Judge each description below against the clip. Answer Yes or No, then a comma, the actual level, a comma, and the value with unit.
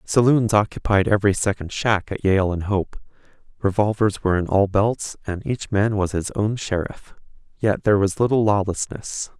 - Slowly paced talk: No, average, 165 wpm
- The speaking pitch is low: Yes, low, 100 Hz